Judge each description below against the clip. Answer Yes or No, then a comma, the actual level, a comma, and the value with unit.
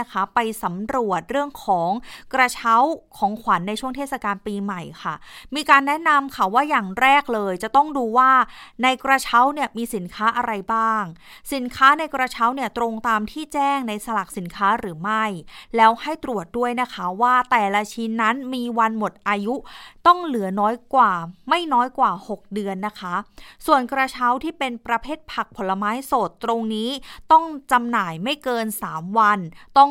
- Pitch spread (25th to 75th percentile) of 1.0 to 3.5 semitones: No, average, 4.2 semitones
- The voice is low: No, high, 235 Hz